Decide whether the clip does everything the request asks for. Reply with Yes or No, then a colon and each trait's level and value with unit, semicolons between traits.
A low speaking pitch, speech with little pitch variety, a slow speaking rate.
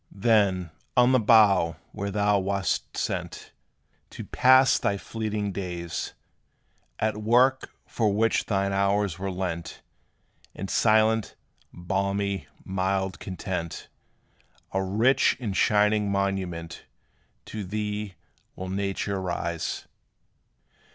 Yes: low, 100 Hz; narrow, 2.2 semitones; slow, 105 wpm